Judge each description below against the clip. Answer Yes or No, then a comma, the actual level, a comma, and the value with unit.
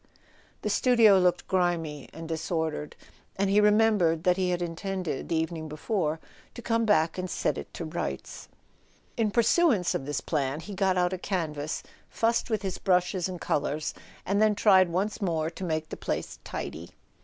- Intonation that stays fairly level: No, average, 4.0 semitones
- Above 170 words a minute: Yes, average, 180 wpm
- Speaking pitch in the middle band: Yes, medium, 180 Hz